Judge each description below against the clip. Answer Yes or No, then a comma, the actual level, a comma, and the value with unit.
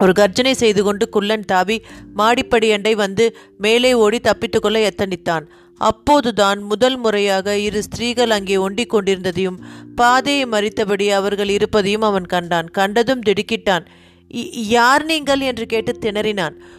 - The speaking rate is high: No, average, 120 wpm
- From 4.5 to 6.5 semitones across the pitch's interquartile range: No, average, 2.7 semitones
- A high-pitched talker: Yes, high, 210 Hz